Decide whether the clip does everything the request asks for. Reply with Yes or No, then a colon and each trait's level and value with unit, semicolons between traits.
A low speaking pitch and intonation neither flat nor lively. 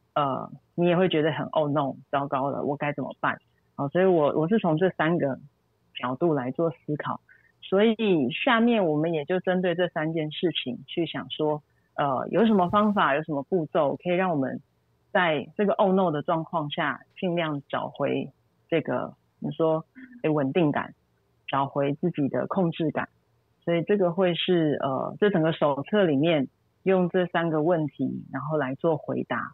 No: medium, 165 Hz; average, 3.7 semitones